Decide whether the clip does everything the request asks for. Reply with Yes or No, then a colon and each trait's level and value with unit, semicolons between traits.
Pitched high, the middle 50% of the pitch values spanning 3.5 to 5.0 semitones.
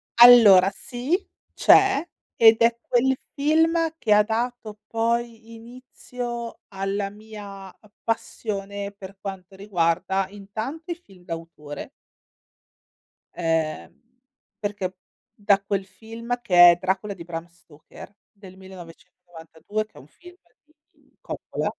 Yes: high, 205 Hz; average, 3.9 semitones